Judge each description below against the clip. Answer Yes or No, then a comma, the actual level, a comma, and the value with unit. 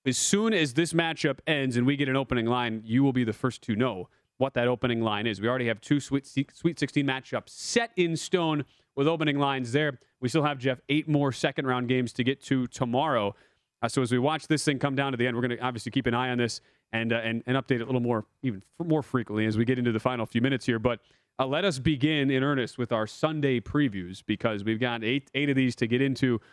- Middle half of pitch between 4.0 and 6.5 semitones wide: No, average, 3.1 semitones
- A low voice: Yes, low, 130 Hz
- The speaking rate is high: Yes, fast, 260 wpm